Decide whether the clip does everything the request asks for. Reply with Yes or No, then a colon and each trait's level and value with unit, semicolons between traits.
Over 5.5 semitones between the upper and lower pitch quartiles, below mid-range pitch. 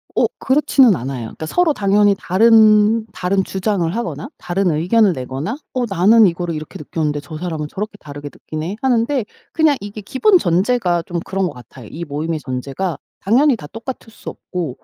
No: wide, 6.3 semitones; high, 190 Hz